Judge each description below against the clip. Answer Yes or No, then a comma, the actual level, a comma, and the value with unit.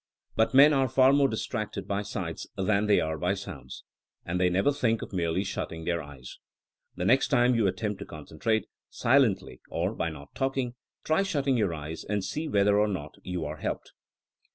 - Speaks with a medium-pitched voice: No, low, 105 Hz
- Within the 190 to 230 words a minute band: Yes, average, 195 wpm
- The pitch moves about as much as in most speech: No, wide, 6.2 semitones